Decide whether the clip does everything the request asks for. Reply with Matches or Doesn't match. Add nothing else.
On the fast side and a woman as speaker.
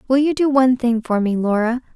Matches